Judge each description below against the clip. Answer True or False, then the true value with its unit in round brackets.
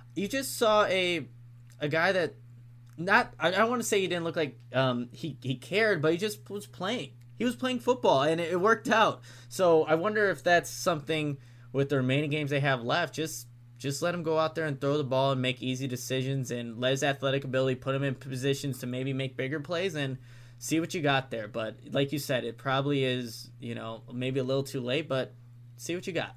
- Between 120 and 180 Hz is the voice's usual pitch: True (135 Hz)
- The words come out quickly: True (230 wpm)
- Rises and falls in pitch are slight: False (4.7 semitones)